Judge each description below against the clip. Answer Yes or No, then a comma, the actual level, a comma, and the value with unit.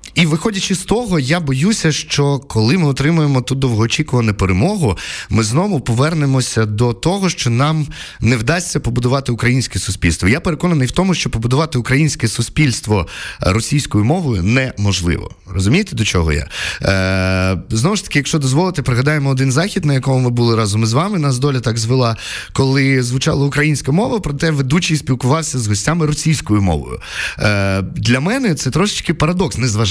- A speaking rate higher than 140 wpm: Yes, fast, 155 wpm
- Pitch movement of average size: No, wide, 5.8 semitones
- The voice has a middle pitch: No, low, 130 Hz